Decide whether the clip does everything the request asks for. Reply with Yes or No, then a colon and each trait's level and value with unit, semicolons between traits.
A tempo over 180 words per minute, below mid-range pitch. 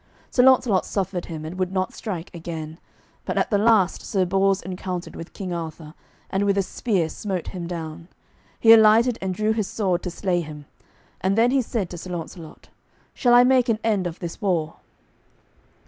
No: average, 190 wpm; medium, 185 Hz